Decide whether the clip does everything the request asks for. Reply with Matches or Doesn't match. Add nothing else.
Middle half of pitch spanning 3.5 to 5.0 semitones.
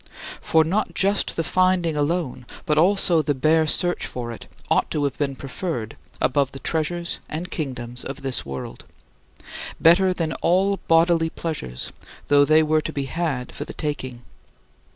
Matches